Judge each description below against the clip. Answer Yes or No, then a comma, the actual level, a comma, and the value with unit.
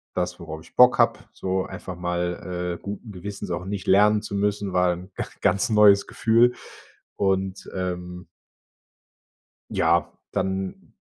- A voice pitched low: Yes, very low, 95 Hz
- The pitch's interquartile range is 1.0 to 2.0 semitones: No, narrow, 2.4 semitones